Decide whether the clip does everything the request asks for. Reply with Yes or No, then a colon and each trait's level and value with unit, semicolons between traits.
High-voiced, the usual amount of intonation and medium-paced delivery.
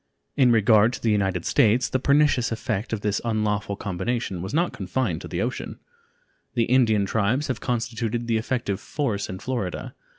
No: low, 115 Hz; average, 3.4 semitones; average, 170 wpm